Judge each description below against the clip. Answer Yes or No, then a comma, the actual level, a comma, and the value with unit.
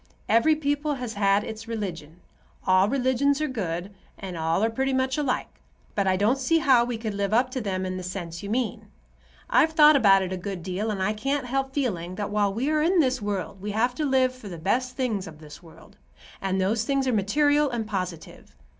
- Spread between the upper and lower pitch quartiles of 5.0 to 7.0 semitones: Yes, wide, 5.6 semitones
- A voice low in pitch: No, high, 220 Hz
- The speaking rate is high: Yes, fast, 220 wpm